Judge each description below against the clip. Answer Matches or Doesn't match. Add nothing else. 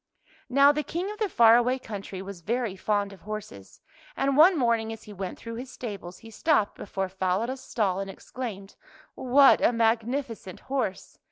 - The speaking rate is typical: Matches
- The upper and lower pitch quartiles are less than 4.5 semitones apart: Doesn't match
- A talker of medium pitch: Doesn't match